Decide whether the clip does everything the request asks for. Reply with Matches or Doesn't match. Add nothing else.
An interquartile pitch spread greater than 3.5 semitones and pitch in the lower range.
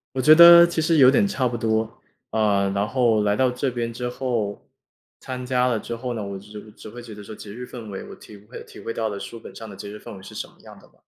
Doesn't match